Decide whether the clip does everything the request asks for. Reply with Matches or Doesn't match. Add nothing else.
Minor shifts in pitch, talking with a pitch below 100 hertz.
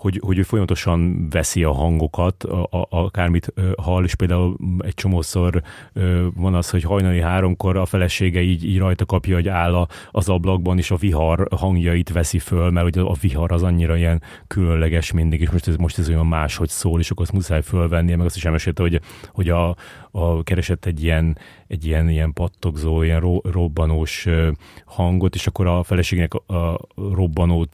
Matches